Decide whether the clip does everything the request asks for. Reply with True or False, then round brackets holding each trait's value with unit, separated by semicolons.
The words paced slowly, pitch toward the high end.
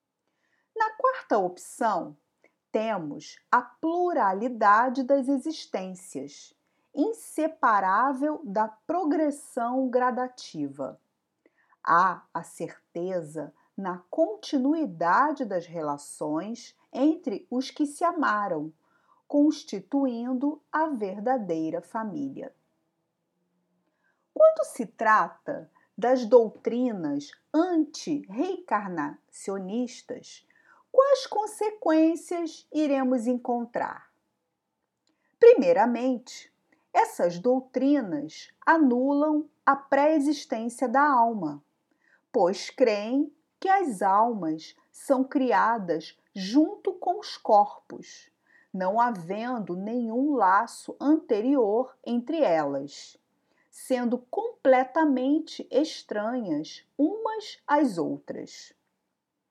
True (70 wpm; 265 Hz)